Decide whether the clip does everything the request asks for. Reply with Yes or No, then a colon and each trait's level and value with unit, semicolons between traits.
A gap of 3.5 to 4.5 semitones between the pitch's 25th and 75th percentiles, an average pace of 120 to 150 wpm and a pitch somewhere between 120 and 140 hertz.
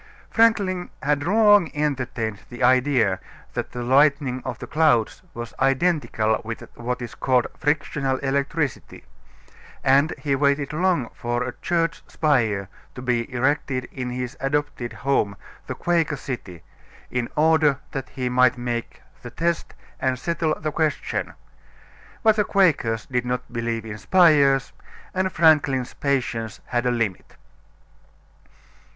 Yes: average, 4.0 semitones; slow, 135 wpm; low, 135 Hz